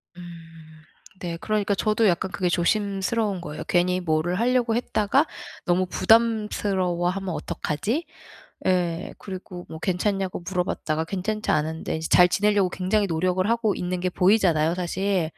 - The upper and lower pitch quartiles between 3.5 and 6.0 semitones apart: No, average, 3.0 semitones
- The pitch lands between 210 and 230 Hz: No, medium, 185 Hz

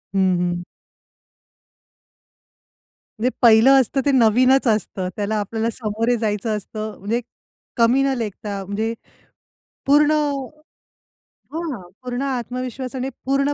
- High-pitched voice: Yes, high, 235 Hz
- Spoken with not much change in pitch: No, average, 3.6 semitones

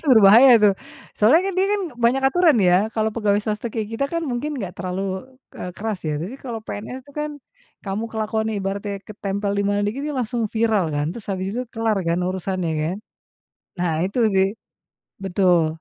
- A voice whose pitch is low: No, high, 210 Hz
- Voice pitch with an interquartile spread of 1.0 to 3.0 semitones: No, average, 3.7 semitones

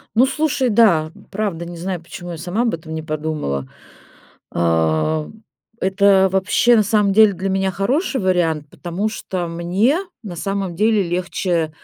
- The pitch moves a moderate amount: Yes, average, 4.0 semitones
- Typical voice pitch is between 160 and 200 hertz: Yes, medium, 185 Hz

